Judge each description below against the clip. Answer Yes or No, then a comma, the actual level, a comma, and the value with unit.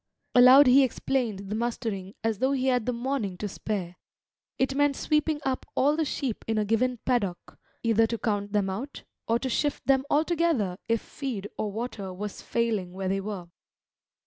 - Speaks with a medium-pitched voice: No, high, 230 Hz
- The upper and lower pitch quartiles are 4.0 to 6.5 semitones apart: Yes, average, 4.6 semitones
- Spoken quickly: No, average, 180 wpm